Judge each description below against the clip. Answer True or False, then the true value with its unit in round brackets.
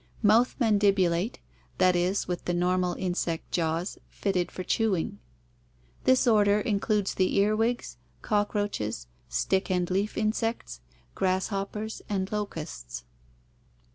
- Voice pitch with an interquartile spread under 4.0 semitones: True (3.0 semitones)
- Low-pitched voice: False (195 Hz)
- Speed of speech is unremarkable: False (110 wpm)